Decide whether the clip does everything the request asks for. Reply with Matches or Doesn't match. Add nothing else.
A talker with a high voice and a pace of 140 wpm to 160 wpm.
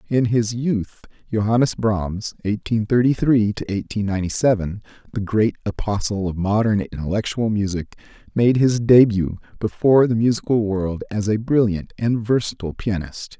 Doesn't match